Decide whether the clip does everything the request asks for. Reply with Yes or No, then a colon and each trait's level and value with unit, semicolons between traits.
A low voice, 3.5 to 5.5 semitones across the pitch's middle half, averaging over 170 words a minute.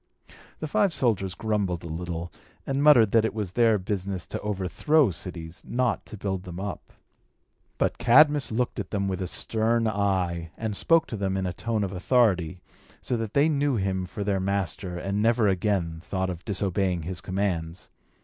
Yes: low, 100 Hz; average, 3.8 semitones; average, 180 wpm